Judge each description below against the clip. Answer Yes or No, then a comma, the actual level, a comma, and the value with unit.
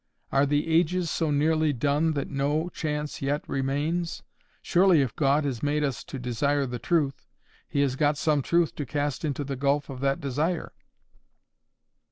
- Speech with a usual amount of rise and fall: No, narrow, 2.2 semitones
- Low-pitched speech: No, medium, 145 Hz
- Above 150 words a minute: Yes, average, 170 wpm